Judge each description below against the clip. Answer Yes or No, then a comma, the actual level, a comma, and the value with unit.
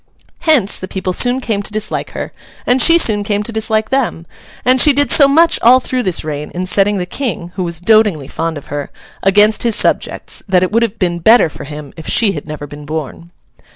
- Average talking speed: No, fast, 225 wpm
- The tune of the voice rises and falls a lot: Yes, wide, 5.7 semitones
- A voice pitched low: No, high, 205 Hz